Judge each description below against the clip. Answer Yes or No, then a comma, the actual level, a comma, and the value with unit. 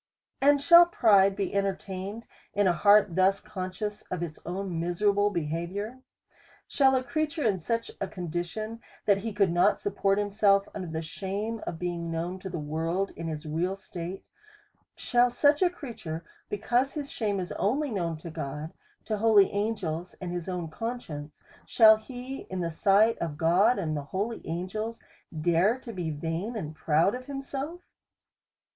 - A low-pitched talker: No, high, 195 Hz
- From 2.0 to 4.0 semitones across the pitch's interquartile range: No, average, 4.8 semitones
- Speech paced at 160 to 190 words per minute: Yes, average, 170 wpm